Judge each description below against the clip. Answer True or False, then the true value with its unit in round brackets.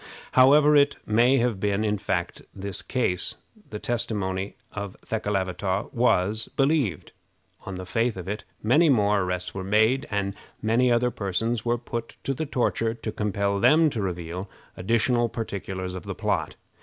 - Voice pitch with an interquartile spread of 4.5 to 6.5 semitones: False (3.9 semitones)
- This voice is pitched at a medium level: False (105 Hz)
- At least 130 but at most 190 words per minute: True (160 wpm)